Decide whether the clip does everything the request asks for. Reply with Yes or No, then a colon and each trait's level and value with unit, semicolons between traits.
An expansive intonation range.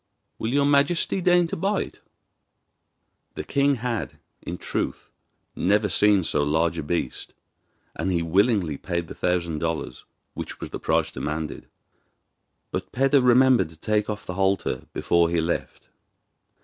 Yes: wide, 7.2 semitones